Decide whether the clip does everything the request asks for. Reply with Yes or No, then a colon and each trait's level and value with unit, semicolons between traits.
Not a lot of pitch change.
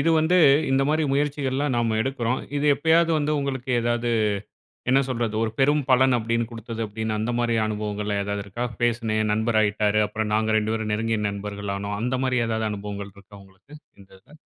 No: average, 3.7 semitones